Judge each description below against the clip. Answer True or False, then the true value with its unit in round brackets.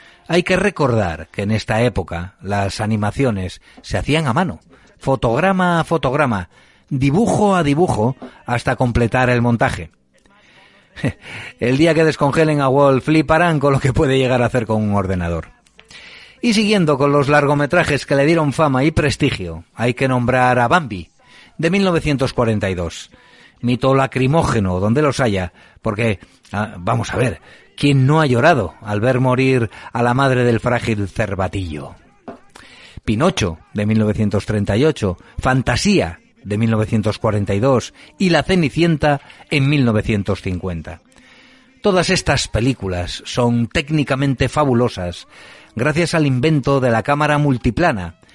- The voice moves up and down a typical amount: False (5.7 semitones)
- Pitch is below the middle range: True (125 Hz)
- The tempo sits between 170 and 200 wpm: False (130 wpm)